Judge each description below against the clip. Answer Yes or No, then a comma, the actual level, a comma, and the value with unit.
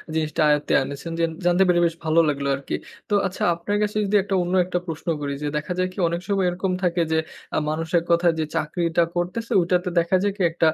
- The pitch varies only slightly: Yes, narrow, 2.3 semitones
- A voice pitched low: No, medium, 170 Hz